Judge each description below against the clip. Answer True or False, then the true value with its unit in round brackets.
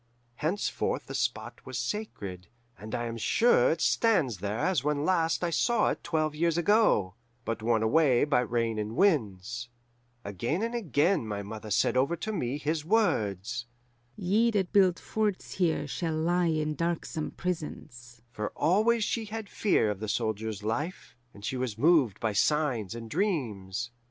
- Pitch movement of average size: False (8.0 semitones)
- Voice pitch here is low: False (145 Hz)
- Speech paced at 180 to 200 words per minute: False (165 wpm)